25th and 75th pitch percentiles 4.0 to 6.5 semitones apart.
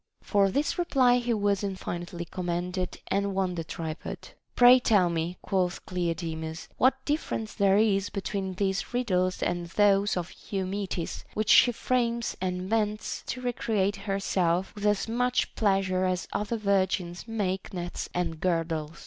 No: average, 3.2 semitones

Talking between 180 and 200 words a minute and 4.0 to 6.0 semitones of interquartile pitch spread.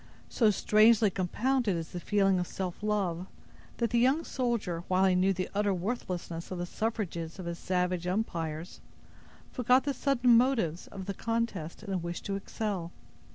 No: average, 170 wpm; average, 4.4 semitones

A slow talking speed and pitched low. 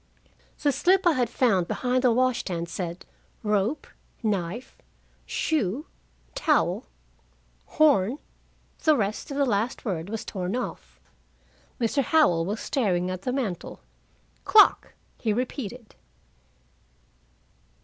No: slow, 120 wpm; high, 230 Hz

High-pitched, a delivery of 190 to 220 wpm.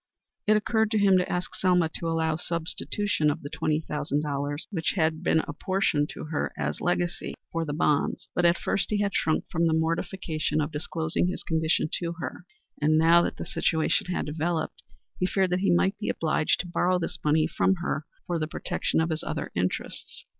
No: medium, 165 Hz; fast, 205 wpm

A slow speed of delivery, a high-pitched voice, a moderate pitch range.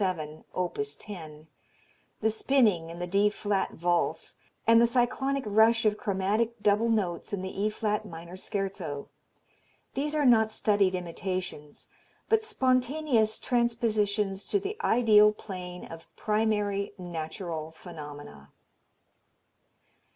Yes: slow, 120 wpm; high, 205 Hz; average, 4.4 semitones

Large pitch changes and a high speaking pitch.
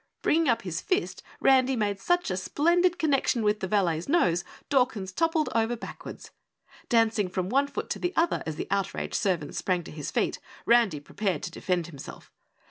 Yes: wide, 7.2 semitones; high, 215 Hz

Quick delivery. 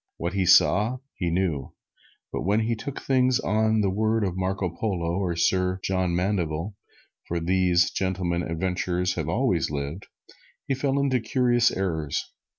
No: average, 155 wpm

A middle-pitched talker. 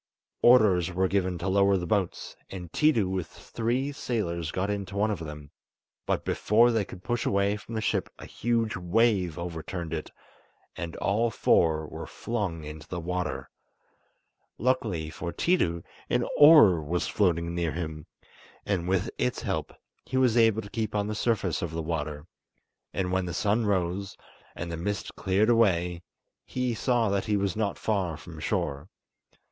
No: very low, 95 Hz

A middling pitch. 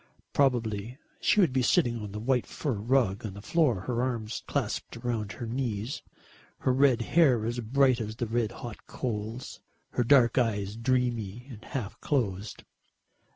No: low, 120 Hz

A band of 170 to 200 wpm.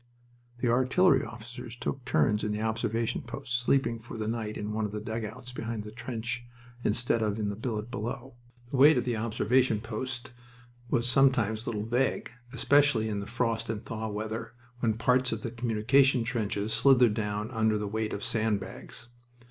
Yes: average, 180 wpm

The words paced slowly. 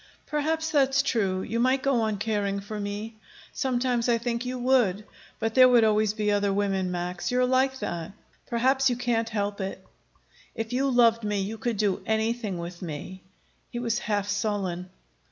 No: average, 175 wpm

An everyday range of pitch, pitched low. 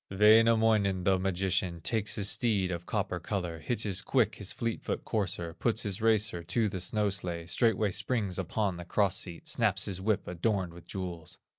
Yes: average, 3.4 semitones; very low, 95 Hz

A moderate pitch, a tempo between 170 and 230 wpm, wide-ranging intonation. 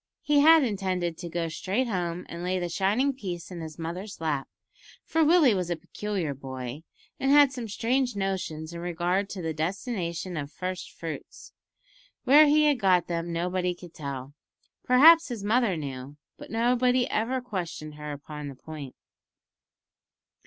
No: medium, 180 Hz; average, 160 wpm; wide, 6.8 semitones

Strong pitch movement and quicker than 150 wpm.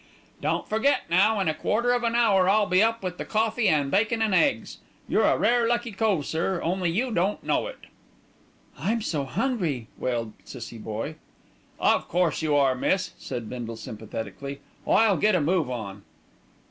Yes: wide, 8.0 semitones; average, 175 wpm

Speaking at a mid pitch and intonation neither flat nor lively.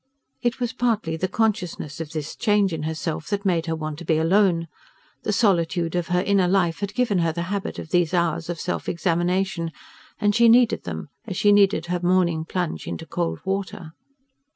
Yes: medium, 180 Hz; average, 3.5 semitones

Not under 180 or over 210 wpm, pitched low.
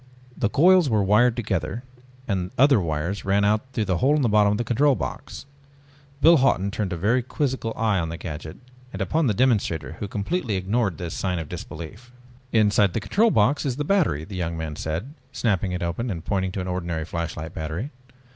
Yes: fast, 205 wpm; low, 100 Hz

